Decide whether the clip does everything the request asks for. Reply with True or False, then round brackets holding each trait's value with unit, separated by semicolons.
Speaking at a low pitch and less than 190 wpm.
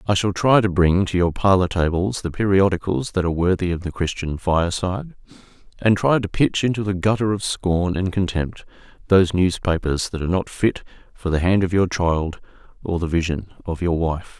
False (90 Hz; 195 wpm)